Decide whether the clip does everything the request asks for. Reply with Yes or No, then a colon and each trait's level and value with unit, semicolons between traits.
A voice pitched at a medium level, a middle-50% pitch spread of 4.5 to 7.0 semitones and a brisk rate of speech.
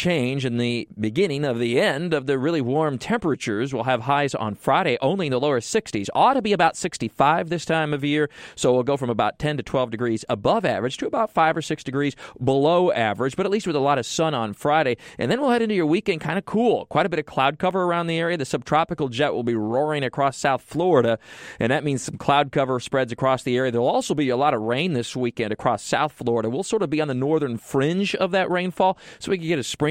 Yes: medium, 145 Hz; average, 5.3 semitones; fast, 255 wpm